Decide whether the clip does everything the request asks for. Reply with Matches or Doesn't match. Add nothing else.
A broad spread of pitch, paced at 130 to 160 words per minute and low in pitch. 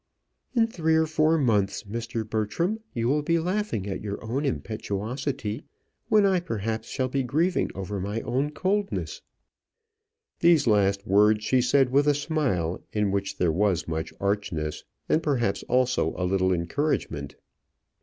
Matches